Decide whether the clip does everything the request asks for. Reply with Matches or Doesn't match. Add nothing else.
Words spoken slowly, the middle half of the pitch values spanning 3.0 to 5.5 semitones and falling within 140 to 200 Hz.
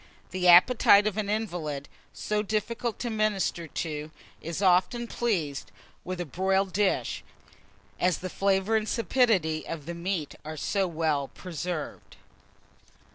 Matches